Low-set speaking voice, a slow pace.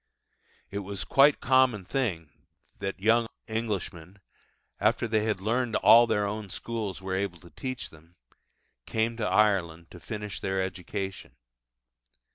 No: low, 105 Hz; average, 145 wpm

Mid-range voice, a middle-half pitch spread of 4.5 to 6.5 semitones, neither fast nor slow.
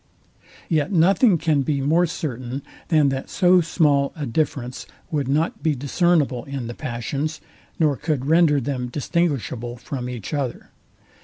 No: medium, 145 Hz; average, 3.8 semitones; average, 145 wpm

